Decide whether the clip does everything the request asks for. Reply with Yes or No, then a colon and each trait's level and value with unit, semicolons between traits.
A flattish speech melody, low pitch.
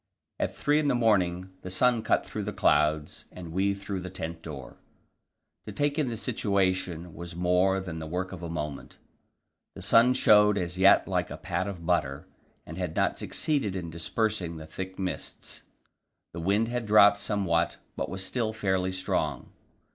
No: average, 3.6 semitones; very low, 95 Hz